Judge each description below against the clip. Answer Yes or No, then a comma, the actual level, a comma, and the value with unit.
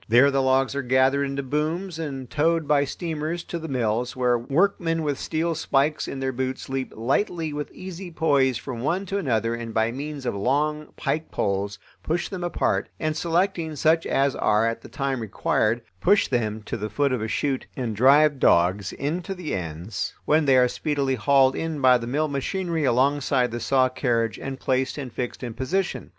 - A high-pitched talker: No, low, 135 Hz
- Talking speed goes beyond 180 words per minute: Yes, average, 190 wpm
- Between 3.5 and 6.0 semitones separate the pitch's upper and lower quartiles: Yes, average, 4.2 semitones